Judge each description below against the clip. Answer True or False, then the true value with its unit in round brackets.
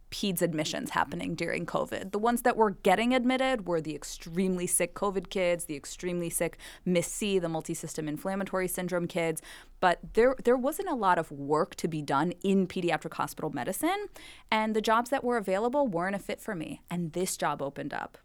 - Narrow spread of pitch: False (4.6 semitones)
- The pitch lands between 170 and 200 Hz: True (185 Hz)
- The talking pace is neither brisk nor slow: True (190 wpm)